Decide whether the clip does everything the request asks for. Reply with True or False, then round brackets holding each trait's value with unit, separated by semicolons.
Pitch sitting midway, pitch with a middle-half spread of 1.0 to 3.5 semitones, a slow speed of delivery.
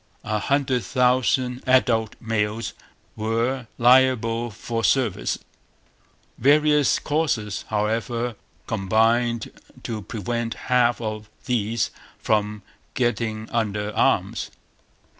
False (115 Hz; 2.6 semitones; 85 wpm)